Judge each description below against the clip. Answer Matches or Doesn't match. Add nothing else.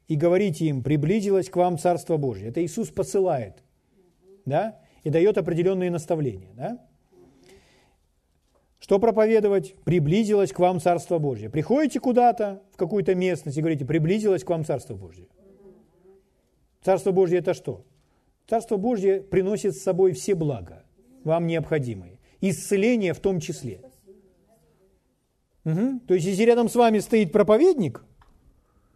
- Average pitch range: Matches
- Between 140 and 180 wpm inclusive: Doesn't match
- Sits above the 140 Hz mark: Matches